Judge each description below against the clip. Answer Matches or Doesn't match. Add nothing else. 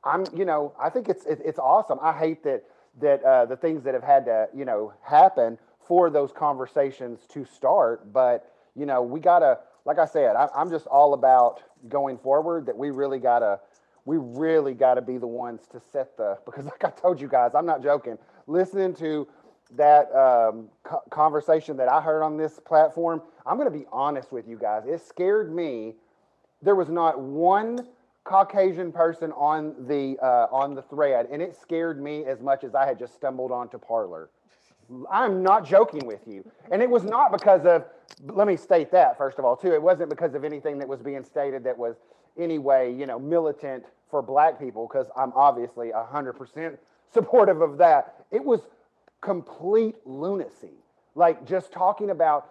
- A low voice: Doesn't match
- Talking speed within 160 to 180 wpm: Doesn't match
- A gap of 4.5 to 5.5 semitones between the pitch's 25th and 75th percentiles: Matches